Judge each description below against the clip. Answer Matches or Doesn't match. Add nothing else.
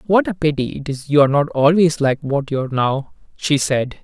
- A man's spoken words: Matches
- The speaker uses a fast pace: Matches